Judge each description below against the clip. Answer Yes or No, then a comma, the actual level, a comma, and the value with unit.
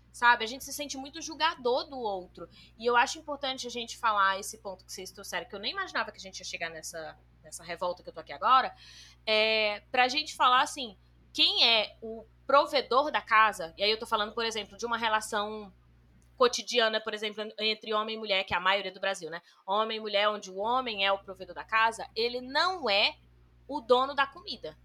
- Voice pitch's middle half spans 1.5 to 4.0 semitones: No, average, 4.6 semitones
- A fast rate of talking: Yes, fast, 220 wpm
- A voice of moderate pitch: No, high, 220 Hz